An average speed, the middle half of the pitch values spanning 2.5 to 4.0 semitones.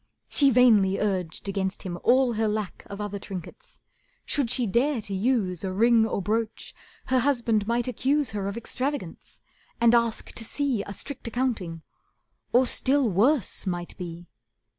No: average, 160 wpm; average, 4.4 semitones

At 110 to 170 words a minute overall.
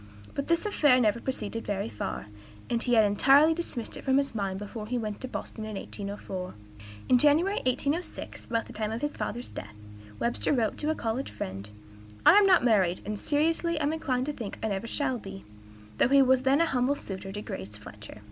No: fast, 205 wpm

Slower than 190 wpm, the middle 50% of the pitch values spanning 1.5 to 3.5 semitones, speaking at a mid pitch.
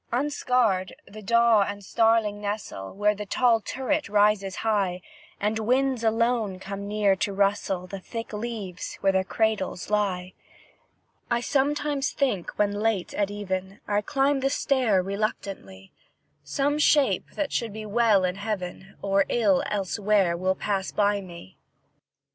No: average, 140 wpm; average, 3.2 semitones; high, 205 Hz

